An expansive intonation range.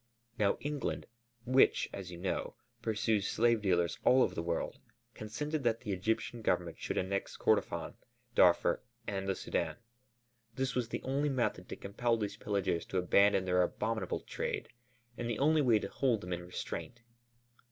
No: average, 4.6 semitones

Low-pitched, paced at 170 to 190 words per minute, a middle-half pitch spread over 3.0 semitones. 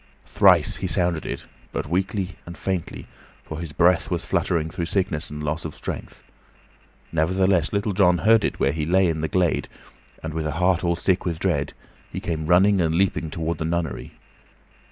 No: very low, 85 Hz; average, 185 wpm; average, 2.7 semitones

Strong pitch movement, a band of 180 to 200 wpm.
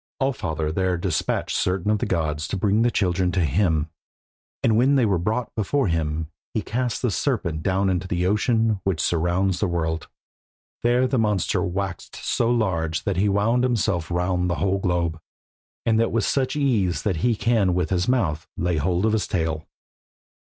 No: average, 4.5 semitones; average, 185 wpm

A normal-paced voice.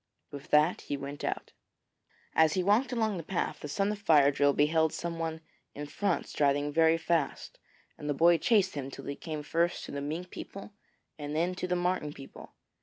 Yes: average, 195 wpm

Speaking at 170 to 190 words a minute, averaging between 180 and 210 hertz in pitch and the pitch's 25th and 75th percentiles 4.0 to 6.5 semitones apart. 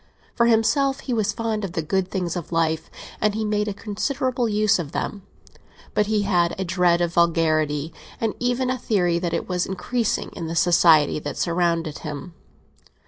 Yes: average, 185 wpm; medium, 185 Hz; average, 4.4 semitones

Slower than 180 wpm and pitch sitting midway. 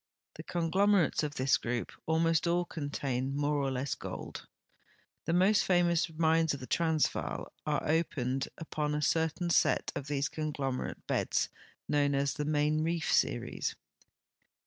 Yes: average, 145 wpm; medium, 150 Hz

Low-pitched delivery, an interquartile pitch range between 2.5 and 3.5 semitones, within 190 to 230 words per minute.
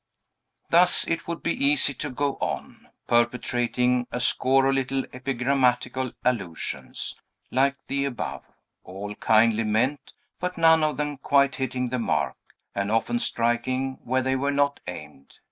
No: low, 130 Hz; average, 2.8 semitones; average, 145 wpm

